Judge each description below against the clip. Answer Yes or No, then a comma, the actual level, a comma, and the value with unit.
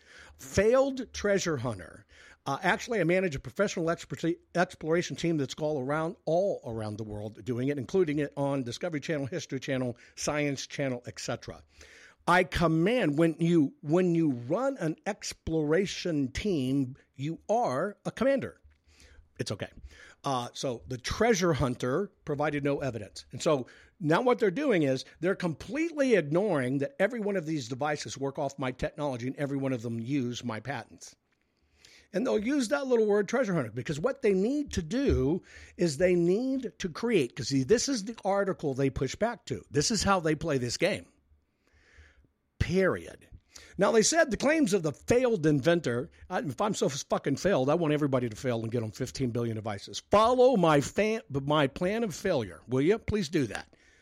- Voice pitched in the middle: Yes, medium, 150 Hz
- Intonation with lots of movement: Yes, wide, 6.7 semitones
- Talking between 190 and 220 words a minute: No, average, 175 wpm